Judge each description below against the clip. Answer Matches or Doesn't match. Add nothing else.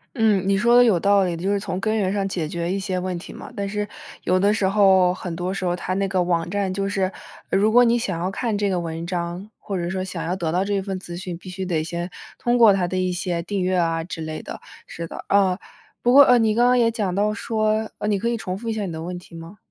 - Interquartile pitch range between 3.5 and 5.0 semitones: Doesn't match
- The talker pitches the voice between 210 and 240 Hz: Doesn't match